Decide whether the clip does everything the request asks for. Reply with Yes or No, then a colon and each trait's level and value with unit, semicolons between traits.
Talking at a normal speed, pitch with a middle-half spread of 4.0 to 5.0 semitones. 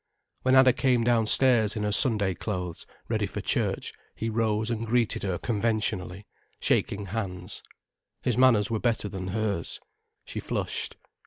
No: average, 145 wpm; average, 2.8 semitones